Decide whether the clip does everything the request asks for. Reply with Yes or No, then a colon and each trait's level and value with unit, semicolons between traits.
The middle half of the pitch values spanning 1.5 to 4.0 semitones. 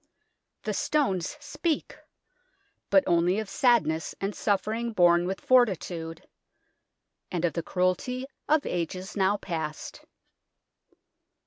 No: wide, 5.4 semitones